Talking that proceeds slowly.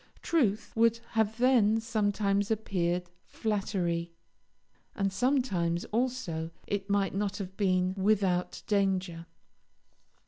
Yes: slow, 100 wpm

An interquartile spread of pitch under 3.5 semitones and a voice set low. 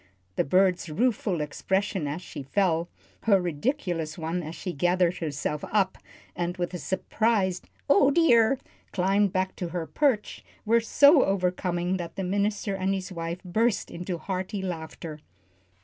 No: average, 3.1 semitones; medium, 185 Hz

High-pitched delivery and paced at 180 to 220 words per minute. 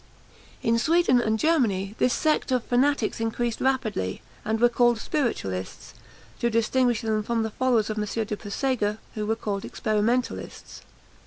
No: high, 230 Hz; average, 150 wpm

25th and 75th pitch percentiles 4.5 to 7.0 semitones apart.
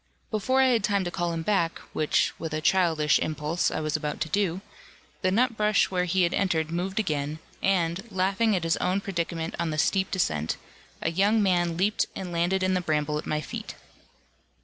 No: average, 3.3 semitones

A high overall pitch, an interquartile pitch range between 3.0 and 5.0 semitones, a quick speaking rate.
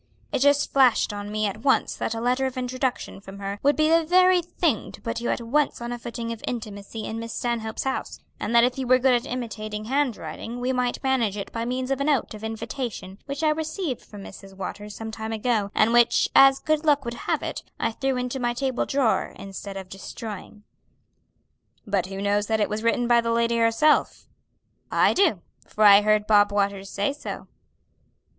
Yes: high, 235 Hz; average, 3.9 semitones; fast, 210 wpm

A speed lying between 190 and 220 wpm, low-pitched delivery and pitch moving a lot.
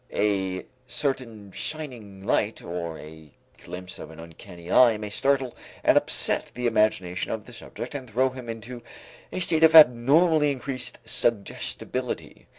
No: average, 145 wpm; low, 115 Hz; wide, 5.7 semitones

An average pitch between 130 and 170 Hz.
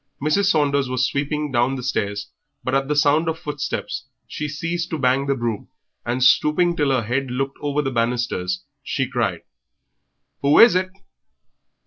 Yes: low, 135 Hz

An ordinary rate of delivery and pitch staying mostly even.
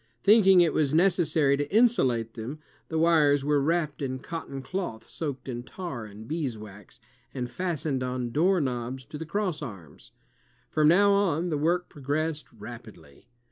No: average, 150 wpm; wide, 5.5 semitones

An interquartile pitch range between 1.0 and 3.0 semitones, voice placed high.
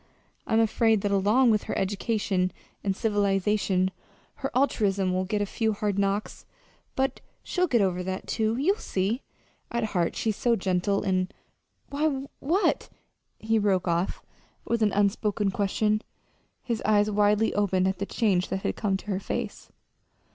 Yes: narrow, 2.6 semitones; high, 205 Hz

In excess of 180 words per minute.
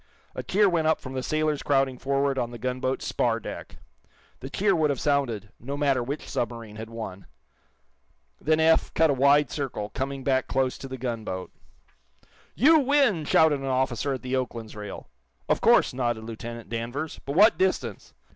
No: average, 175 wpm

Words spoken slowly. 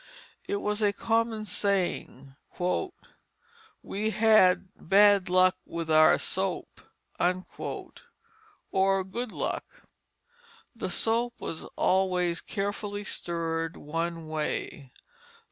Yes: slow, 90 wpm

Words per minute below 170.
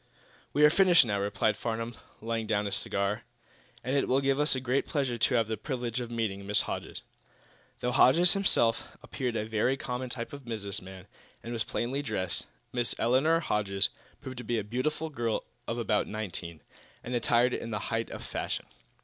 No: average, 190 wpm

